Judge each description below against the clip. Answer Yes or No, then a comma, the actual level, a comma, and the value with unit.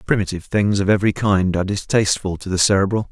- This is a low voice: Yes, low, 100 Hz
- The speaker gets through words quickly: No, average, 190 wpm